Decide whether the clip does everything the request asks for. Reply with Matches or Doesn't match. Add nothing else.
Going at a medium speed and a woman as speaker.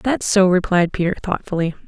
Matches